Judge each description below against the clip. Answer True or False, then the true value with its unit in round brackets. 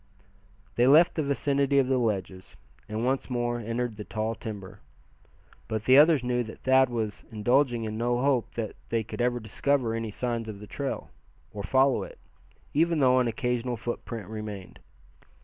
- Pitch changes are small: False (3.2 semitones)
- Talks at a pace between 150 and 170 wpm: True (165 wpm)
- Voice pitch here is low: True (120 Hz)